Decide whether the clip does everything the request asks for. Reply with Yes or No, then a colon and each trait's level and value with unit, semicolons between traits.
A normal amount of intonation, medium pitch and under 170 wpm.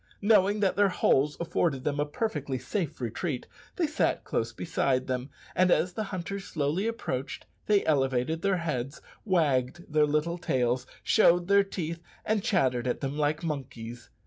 No: wide, 6.0 semitones; medium, 155 Hz; average, 160 wpm